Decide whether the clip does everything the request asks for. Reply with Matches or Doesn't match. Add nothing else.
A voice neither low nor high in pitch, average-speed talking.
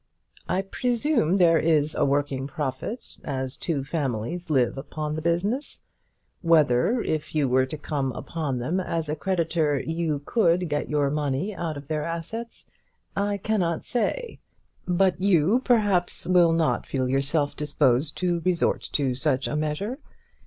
Matches